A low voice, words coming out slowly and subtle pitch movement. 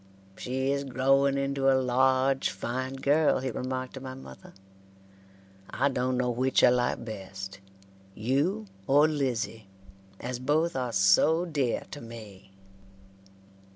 Yes: low, 130 Hz; slow, 130 wpm; narrow, 2.2 semitones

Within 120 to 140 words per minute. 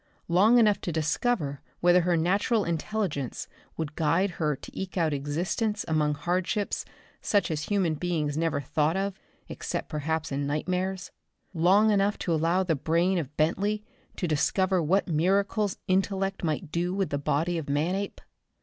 No: average, 155 wpm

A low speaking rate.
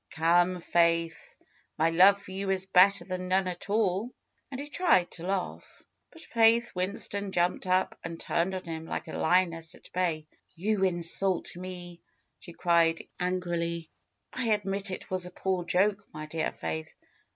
No: average, 160 wpm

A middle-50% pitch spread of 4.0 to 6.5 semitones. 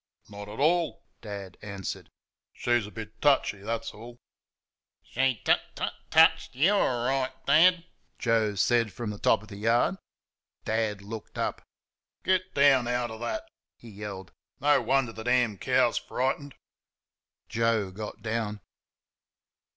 Yes: average, 4.3 semitones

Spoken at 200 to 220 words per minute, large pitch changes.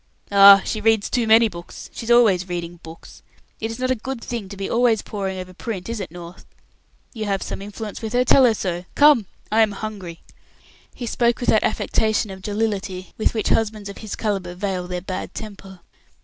No: fast, 205 wpm; average, 3.2 semitones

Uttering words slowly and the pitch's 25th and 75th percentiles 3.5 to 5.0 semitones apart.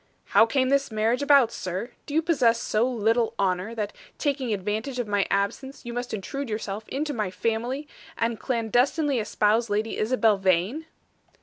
No: average, 165 wpm; average, 3.9 semitones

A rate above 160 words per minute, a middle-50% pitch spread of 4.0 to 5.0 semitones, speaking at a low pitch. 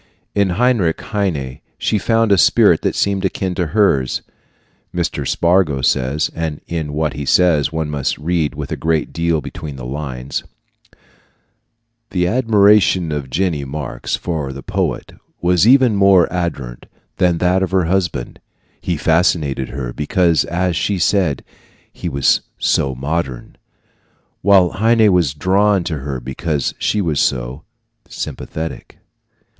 No: average, 140 wpm; average, 4.7 semitones; very low, 85 Hz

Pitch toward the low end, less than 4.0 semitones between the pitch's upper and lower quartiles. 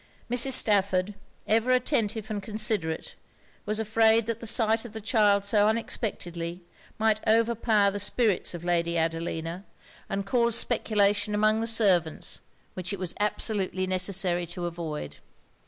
No: high, 205 Hz; average, 3.5 semitones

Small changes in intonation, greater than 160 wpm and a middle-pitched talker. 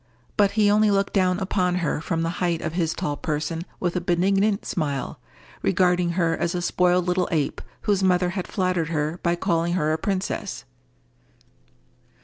Yes: narrow, 2.2 semitones; average, 170 wpm; medium, 180 Hz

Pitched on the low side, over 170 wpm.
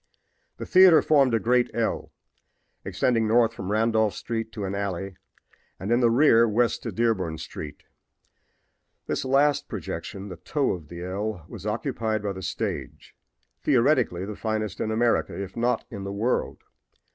No: low, 110 Hz; average, 155 wpm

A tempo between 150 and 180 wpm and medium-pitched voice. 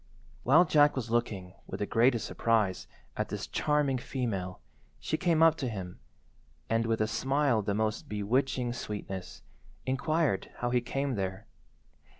No: average, 155 wpm; low, 120 Hz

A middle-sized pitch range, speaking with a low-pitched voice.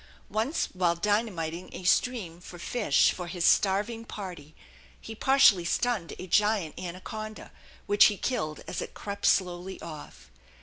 No: average, 3.9 semitones; high, 190 Hz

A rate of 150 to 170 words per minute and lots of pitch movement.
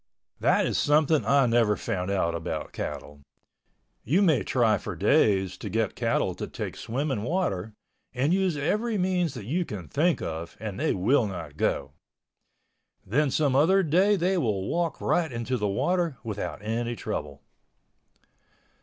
Yes: average, 155 wpm; wide, 8.5 semitones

